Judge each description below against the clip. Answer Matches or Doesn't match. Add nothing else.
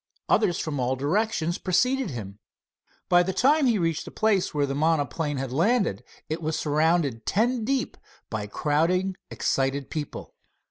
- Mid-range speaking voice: Matches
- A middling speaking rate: Matches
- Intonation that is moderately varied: Doesn't match